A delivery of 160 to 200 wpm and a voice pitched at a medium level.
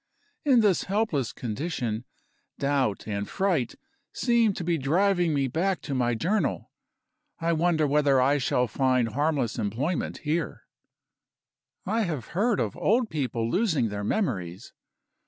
No: slow, 135 wpm; medium, 150 Hz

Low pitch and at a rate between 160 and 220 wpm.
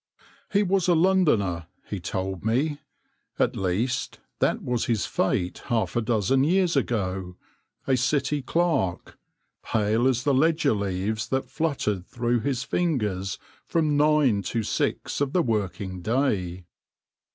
No: low, 120 Hz; average, 145 wpm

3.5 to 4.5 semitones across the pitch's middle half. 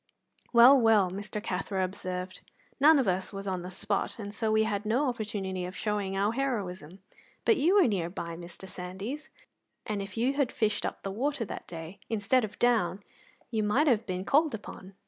Yes: average, 3.9 semitones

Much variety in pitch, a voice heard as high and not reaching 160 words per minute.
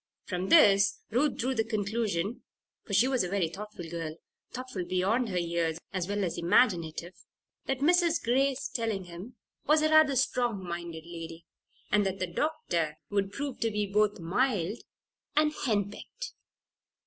Yes: wide, 6.4 semitones; high, 205 Hz; average, 150 wpm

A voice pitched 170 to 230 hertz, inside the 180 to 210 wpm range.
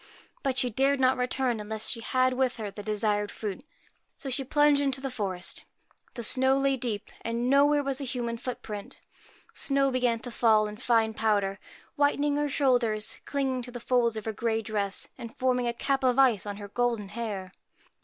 No: high, 245 Hz; average, 190 wpm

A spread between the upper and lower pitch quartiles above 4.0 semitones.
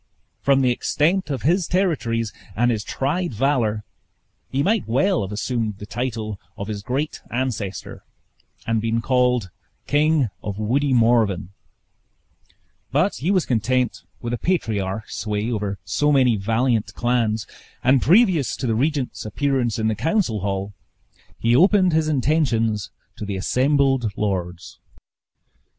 Yes: average, 4.9 semitones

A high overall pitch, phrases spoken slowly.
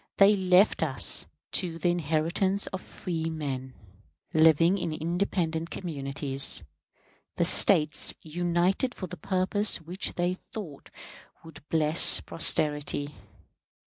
No: medium, 165 Hz; slow, 105 wpm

